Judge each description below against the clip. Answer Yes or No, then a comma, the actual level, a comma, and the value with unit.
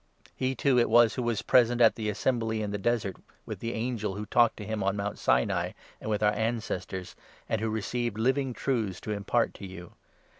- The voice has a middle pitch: No, low, 110 Hz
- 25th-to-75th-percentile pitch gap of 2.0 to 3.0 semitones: Yes, average, 2.7 semitones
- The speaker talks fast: Yes, fast, 215 wpm